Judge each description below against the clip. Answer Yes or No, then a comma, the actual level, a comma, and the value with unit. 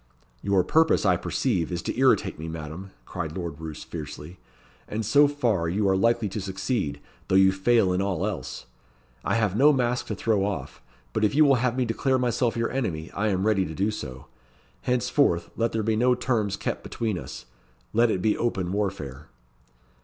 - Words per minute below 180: No, average, 190 wpm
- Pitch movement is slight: No, average, 4.7 semitones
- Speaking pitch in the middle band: No, low, 100 Hz